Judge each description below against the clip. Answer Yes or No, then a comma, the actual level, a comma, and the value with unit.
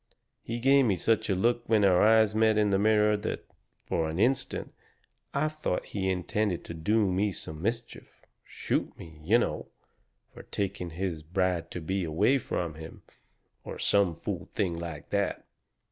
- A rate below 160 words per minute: No, average, 175 wpm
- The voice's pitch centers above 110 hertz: No, low, 100 Hz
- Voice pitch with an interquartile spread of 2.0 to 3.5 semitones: No, average, 4.4 semitones